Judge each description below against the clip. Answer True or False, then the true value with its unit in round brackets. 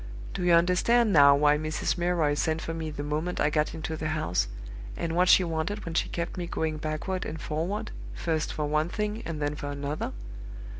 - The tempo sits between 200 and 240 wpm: True (205 wpm)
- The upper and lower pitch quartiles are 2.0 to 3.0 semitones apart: True (2.6 semitones)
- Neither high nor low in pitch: True (160 Hz)